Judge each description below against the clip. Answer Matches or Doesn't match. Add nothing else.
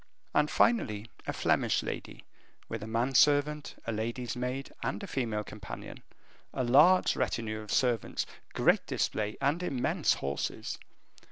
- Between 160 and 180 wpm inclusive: Doesn't match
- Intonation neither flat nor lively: Matches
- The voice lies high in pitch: Doesn't match